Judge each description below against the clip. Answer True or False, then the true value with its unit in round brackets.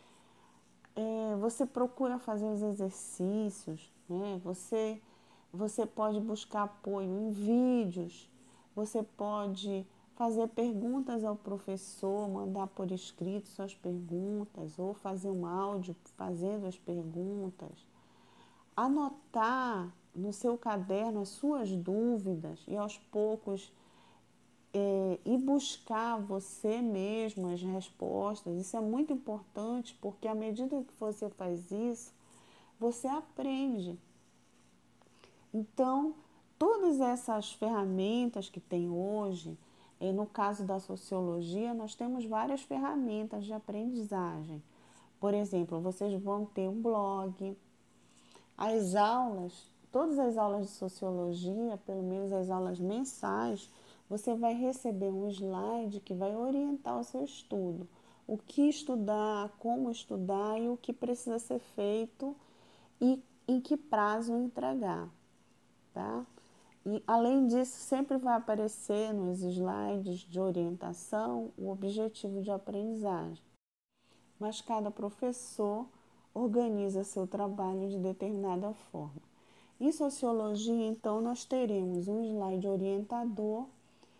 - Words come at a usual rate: False (115 wpm)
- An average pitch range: True (3.5 semitones)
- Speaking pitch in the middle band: False (210 Hz)